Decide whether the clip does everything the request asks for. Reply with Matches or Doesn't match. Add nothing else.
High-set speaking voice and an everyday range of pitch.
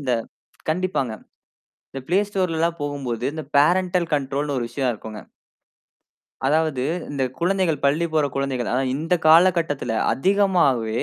Doesn't match